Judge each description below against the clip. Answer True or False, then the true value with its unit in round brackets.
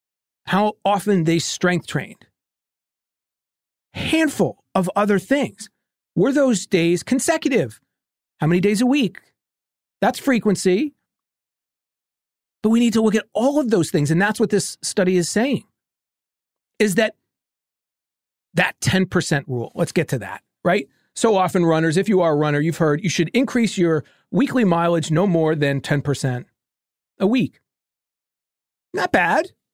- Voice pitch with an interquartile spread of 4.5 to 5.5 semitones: True (5.0 semitones)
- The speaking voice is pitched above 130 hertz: True (185 Hz)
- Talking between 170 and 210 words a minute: False (145 wpm)